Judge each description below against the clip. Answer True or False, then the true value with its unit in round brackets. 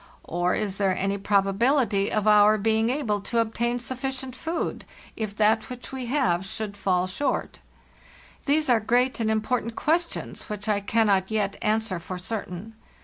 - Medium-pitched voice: False (215 Hz)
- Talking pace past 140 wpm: True (165 wpm)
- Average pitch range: True (3.5 semitones)